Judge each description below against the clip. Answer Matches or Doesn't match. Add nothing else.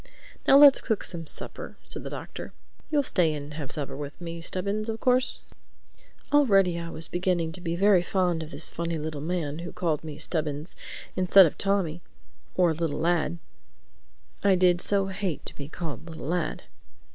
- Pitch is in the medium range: Matches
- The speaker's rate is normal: Matches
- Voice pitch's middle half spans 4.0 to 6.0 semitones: Doesn't match